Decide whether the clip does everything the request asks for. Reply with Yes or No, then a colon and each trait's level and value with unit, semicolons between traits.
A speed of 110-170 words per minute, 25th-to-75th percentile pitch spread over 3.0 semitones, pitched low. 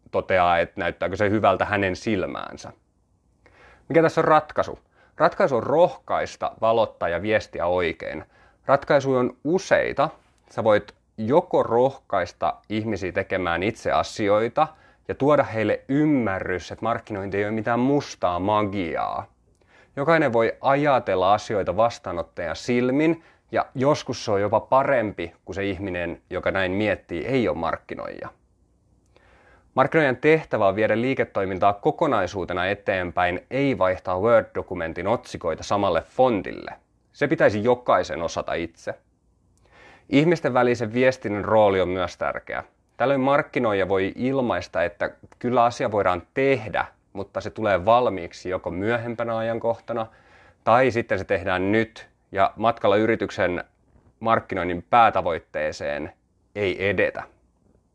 Yes: average, 120 wpm; average, 4.7 semitones; low, 110 Hz